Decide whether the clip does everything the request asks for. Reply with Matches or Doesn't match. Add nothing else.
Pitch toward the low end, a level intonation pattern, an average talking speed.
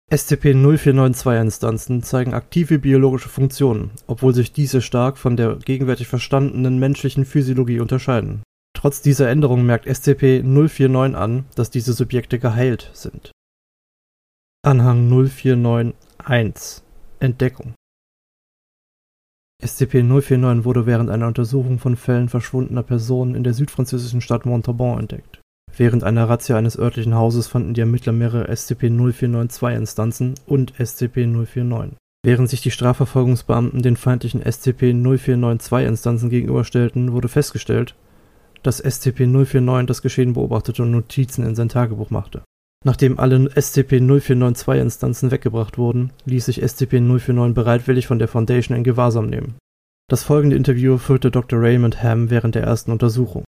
Doesn't match